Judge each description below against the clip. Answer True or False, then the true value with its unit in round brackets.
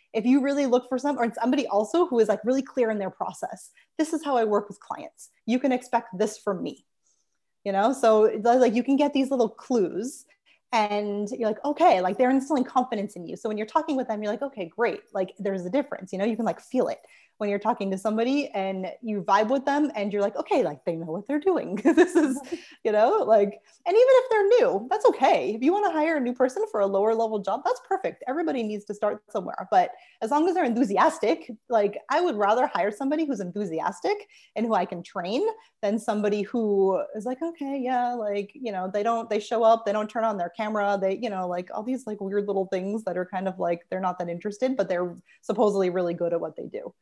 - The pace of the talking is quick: True (245 wpm)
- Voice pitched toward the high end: True (225 Hz)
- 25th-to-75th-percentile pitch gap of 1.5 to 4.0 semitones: False (5.3 semitones)